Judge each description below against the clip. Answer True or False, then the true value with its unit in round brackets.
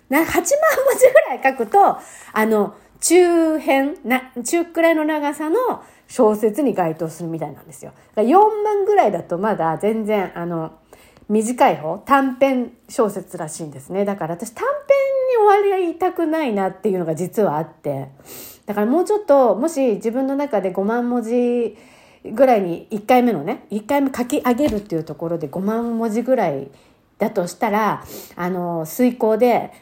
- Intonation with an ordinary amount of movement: False (7.2 semitones)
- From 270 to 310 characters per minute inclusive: True (305 characters per minute)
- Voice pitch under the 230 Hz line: False (235 Hz)